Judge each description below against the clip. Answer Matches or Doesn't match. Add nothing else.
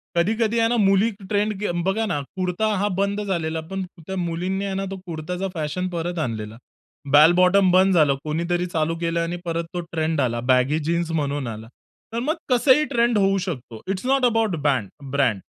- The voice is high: Doesn't match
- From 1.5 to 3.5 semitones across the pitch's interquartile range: Doesn't match